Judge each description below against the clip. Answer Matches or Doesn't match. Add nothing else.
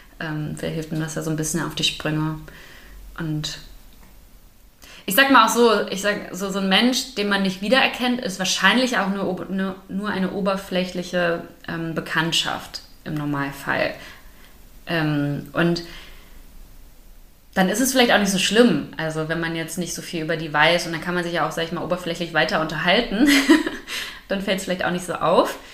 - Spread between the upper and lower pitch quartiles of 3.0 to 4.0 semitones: Matches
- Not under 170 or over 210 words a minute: Matches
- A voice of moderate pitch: Matches